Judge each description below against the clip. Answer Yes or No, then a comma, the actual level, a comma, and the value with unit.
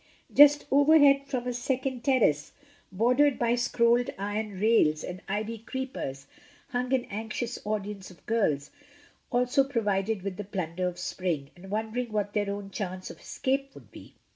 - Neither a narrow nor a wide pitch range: Yes, average, 4.5 semitones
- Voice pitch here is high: Yes, high, 220 Hz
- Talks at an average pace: Yes, average, 155 wpm